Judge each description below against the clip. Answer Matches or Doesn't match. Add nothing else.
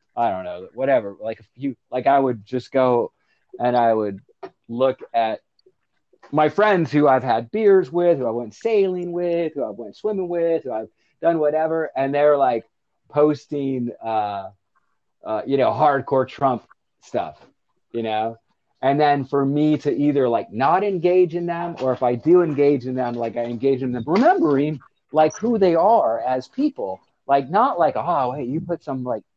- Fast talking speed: Doesn't match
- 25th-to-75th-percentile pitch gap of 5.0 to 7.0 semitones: Matches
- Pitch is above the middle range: Doesn't match